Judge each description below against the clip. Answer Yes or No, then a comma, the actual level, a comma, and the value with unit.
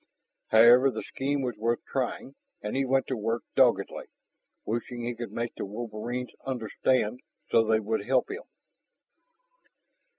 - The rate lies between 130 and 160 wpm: Yes, average, 140 wpm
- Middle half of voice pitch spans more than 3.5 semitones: No, narrow, 2.5 semitones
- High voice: No, low, 120 Hz